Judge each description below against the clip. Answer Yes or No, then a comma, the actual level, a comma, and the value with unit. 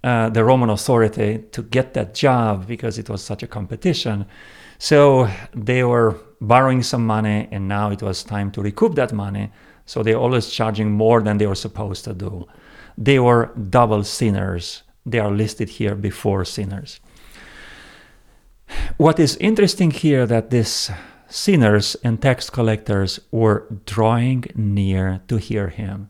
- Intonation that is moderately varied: Yes, average, 3.0 semitones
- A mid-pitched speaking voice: No, low, 110 Hz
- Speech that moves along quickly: No, average, 150 wpm